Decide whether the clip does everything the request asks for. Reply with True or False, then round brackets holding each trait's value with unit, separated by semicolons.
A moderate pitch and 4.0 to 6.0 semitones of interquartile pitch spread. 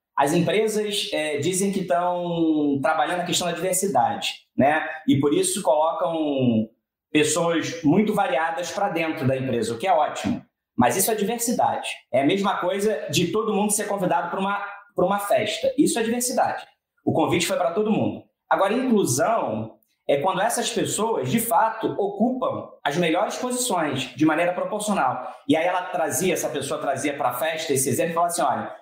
True (180 Hz; 4.7 semitones)